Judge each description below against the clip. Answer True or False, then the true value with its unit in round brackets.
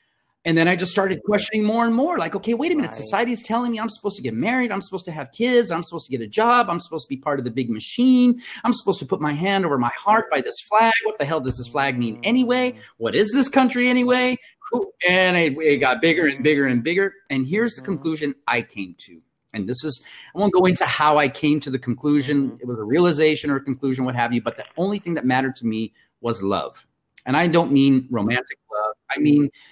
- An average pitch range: False (8.5 semitones)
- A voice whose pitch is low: False (165 Hz)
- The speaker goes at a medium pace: False (250 wpm)